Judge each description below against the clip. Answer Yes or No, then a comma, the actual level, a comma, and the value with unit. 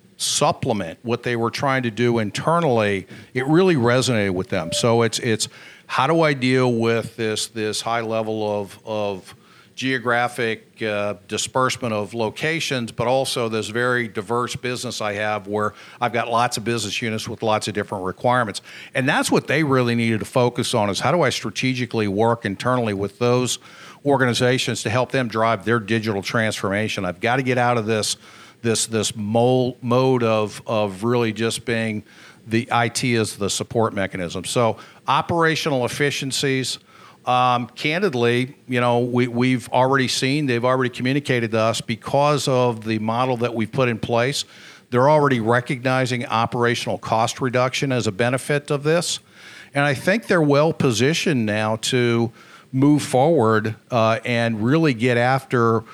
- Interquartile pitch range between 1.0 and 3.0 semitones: Yes, average, 2.7 semitones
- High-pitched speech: No, low, 120 Hz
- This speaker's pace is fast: No, average, 160 wpm